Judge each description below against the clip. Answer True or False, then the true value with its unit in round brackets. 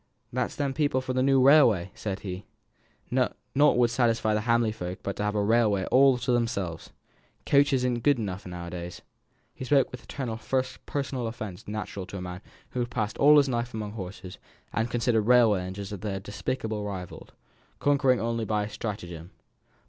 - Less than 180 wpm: False (185 wpm)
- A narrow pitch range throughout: False (4.2 semitones)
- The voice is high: False (115 Hz)